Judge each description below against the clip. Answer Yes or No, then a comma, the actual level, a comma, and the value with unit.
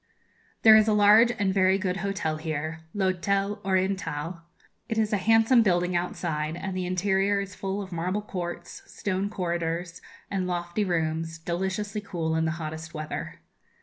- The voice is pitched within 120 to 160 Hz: No, medium, 185 Hz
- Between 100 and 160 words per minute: Yes, average, 155 wpm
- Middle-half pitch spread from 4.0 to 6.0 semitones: No, average, 3.1 semitones